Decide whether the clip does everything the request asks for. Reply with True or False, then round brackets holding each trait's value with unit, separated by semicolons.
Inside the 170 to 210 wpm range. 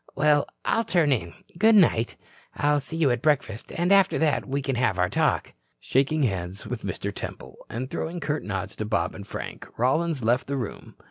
True (195 wpm)